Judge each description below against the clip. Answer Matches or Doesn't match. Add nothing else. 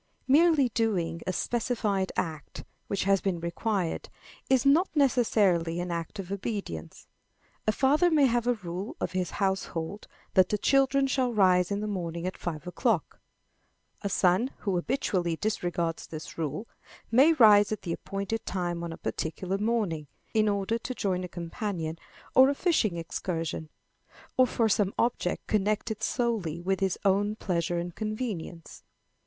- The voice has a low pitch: Doesn't match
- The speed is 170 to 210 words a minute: Doesn't match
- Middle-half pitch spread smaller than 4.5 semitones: Doesn't match